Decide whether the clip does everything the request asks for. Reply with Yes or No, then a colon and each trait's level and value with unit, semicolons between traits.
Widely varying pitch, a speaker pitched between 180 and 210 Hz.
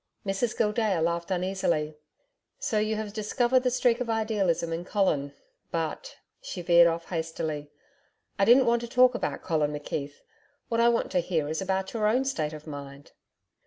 Yes: wide, 6.0 semitones; high, 190 Hz